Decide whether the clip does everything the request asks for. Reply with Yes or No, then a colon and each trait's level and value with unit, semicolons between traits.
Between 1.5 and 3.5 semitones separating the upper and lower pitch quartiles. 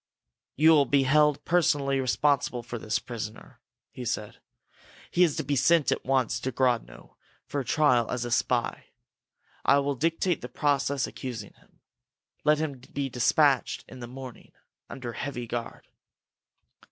Yes: average, 3.0 semitones